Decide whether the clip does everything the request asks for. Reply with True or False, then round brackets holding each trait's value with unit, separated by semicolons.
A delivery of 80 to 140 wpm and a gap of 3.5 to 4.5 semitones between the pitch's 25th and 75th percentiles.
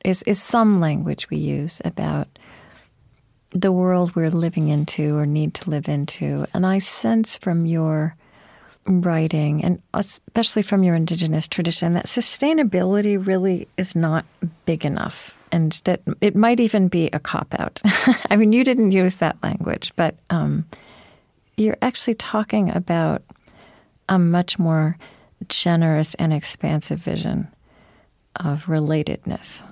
True (135 wpm; 4.2 semitones)